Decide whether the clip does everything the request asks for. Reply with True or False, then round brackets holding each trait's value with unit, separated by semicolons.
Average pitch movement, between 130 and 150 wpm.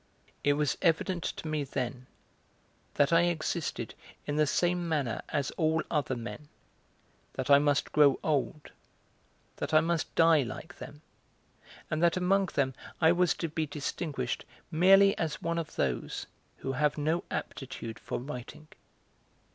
True (3.1 semitones; 145 wpm)